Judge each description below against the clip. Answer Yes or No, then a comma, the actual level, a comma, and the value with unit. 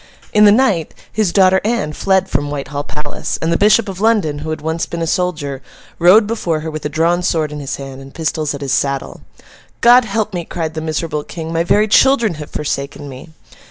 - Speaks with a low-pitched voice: No, medium, 165 Hz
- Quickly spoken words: Yes, fast, 215 wpm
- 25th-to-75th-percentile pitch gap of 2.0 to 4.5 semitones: No, average, 4.9 semitones